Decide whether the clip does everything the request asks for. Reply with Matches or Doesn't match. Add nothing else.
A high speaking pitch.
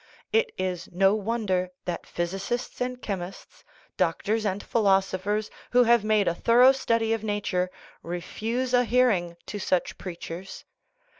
Matches